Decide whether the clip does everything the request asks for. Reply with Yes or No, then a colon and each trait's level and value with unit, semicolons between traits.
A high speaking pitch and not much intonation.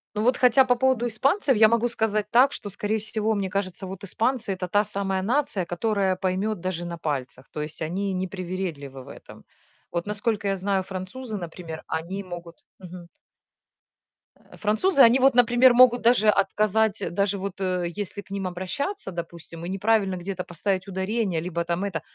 No: high, 195 Hz; average, 3.4 semitones